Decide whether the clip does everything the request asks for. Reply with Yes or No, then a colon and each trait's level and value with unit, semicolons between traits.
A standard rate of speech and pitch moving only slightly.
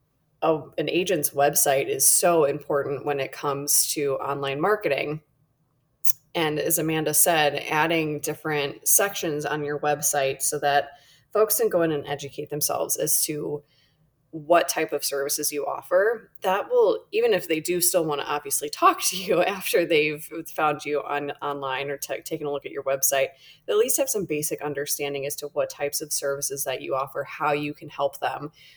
Yes: average, 180 wpm; narrow, 1.9 semitones